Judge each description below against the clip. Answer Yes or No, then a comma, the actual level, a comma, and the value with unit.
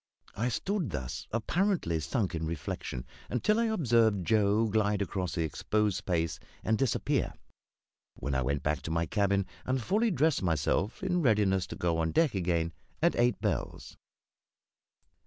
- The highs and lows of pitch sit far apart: Yes, wide, 7.1 semitones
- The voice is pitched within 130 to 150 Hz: No, low, 100 Hz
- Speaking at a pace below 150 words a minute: No, average, 155 wpm